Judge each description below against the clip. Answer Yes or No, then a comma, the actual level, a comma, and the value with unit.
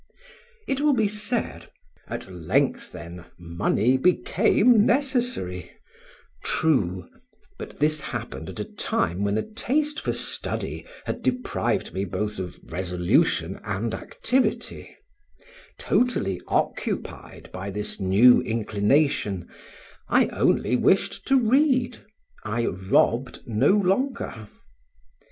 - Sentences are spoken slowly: Yes, slow, 105 wpm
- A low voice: Yes, low, 120 Hz